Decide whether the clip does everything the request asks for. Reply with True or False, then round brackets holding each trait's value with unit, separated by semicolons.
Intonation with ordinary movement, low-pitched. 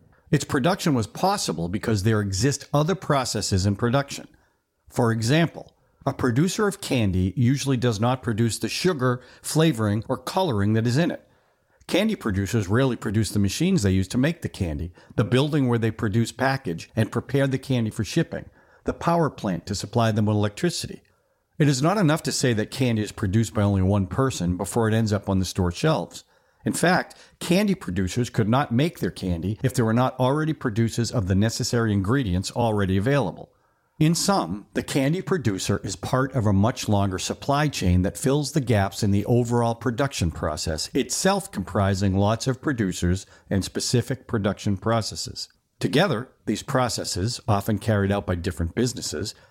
True (5.0 semitones; 115 Hz)